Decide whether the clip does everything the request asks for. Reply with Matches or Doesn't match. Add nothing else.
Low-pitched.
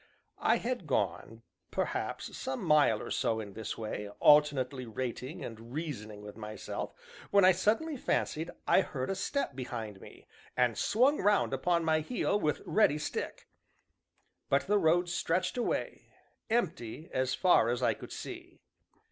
Doesn't match